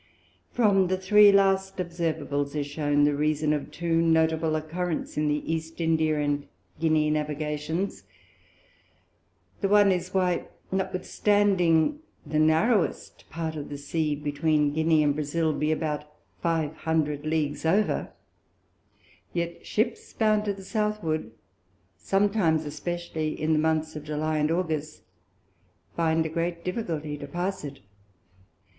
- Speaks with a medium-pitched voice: Yes, medium, 160 Hz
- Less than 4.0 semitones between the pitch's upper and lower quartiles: Yes, average, 3.0 semitones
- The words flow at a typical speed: No, slow, 130 wpm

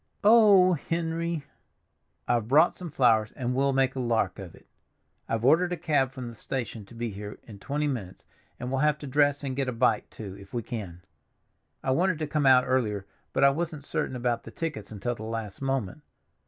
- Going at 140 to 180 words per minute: No, fast, 205 wpm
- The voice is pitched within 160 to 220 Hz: No, low, 130 Hz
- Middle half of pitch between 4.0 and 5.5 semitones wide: Yes, average, 4.8 semitones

